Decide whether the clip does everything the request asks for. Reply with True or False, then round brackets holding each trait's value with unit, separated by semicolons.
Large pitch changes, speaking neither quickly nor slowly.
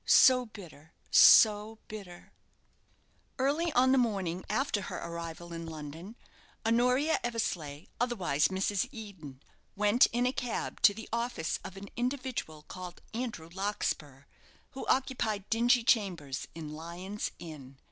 False (6.3 semitones; 125 wpm)